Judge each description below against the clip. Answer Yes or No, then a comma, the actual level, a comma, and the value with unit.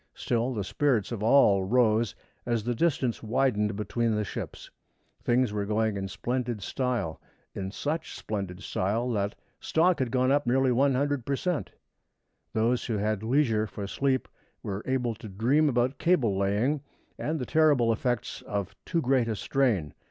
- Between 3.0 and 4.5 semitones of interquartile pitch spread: Yes, average, 4.0 semitones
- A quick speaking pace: No, average, 160 wpm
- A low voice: Yes, low, 120 Hz